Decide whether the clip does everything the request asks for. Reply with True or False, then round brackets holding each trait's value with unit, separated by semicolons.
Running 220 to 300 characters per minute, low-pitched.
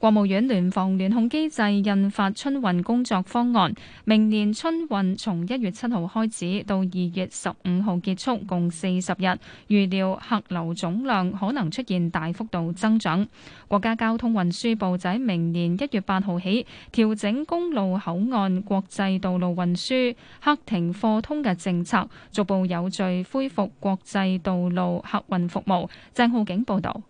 False (240 characters per minute; 195 Hz)